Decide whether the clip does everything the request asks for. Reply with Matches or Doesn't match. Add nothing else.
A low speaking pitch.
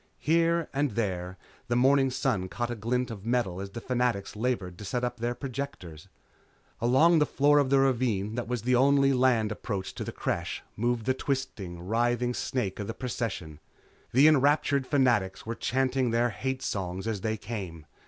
Matches